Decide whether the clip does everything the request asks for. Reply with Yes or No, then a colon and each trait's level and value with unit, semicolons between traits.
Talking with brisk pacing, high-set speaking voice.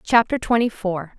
No: average, 150 wpm; high, 210 Hz